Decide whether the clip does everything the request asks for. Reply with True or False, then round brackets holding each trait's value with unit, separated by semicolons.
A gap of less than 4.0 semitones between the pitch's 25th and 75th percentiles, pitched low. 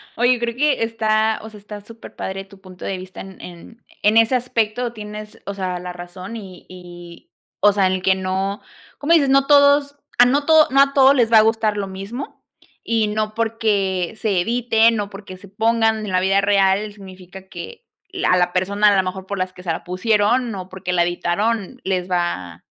False (3.6 semitones; 205 Hz)